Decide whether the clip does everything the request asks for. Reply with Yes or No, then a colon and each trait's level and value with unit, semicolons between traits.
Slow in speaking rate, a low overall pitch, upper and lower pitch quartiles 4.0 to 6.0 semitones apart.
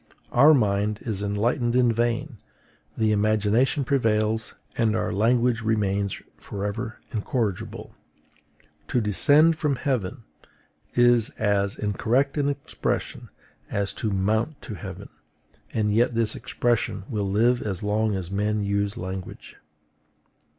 No: slow, 120 wpm; low, 110 Hz; average, 3.0 semitones